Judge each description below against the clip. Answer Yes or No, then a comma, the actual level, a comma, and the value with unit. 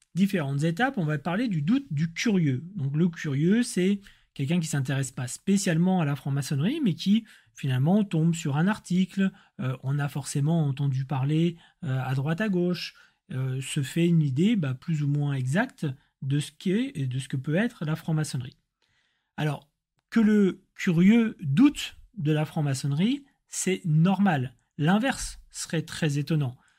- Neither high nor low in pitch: Yes, medium, 160 Hz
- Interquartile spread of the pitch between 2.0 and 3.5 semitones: No, average, 5.0 semitones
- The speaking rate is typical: Yes, average, 170 wpm